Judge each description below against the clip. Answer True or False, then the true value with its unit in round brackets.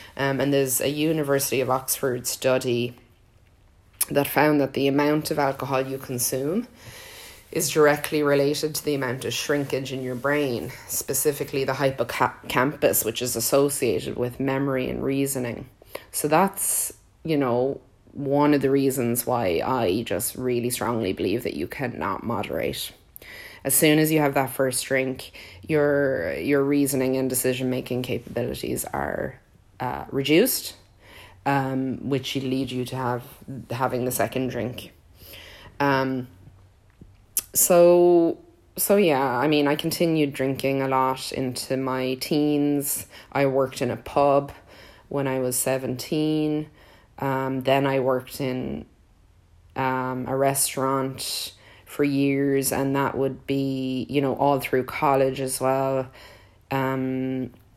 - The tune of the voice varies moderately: False (2.1 semitones)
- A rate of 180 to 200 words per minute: False (135 wpm)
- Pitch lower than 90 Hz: False (130 Hz)